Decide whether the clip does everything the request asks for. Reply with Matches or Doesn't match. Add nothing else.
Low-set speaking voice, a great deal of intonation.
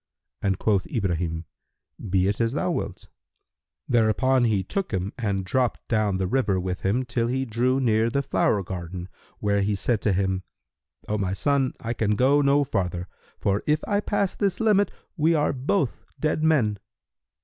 Matches